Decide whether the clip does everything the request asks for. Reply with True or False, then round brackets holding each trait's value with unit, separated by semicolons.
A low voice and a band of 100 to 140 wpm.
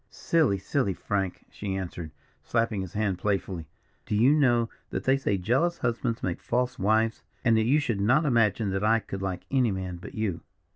False (110 Hz; 190 wpm)